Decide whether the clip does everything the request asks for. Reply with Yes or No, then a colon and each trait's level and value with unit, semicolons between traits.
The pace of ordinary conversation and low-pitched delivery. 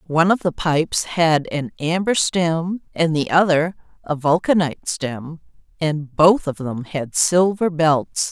No: average, 150 wpm; medium, 165 Hz